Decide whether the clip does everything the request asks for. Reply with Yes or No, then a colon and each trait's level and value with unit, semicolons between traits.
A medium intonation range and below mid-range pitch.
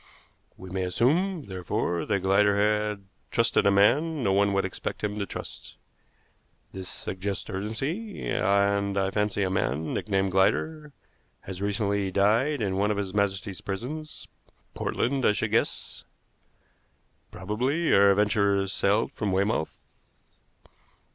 No: narrow, 2.2 semitones; low, 100 Hz